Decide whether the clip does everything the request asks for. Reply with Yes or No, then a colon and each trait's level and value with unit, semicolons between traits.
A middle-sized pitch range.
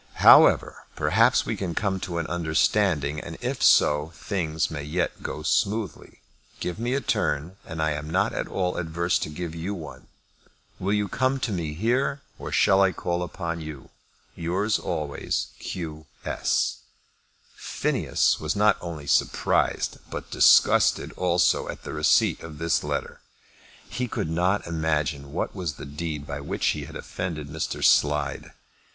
Yes: average, 3.8 semitones